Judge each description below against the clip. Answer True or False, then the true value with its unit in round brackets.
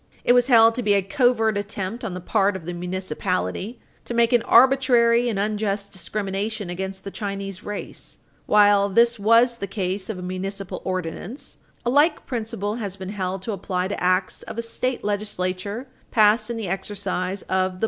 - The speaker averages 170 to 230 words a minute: True (190 wpm)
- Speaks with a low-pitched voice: False (205 Hz)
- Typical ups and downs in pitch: True (3.4 semitones)